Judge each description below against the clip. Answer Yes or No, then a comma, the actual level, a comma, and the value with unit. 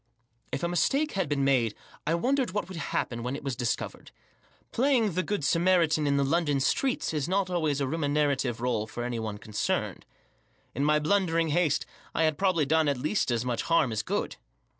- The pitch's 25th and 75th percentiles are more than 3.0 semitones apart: Yes, average, 5.0 semitones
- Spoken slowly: No, average, 195 wpm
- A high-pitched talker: No, medium, 150 Hz